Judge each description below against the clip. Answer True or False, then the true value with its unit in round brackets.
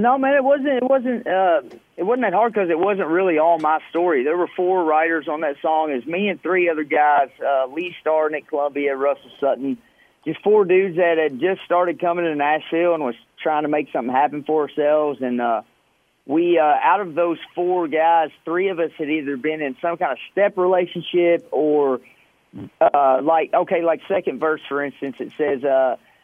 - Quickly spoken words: True (210 wpm)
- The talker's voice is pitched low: False (165 Hz)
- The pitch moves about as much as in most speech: True (3.4 semitones)